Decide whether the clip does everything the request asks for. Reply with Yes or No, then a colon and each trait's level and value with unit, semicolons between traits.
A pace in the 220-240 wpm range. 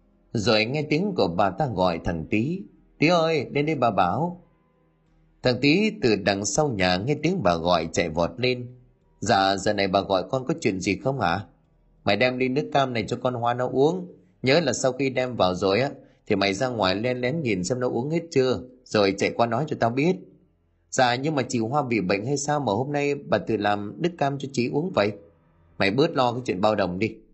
Yes: average, 235 wpm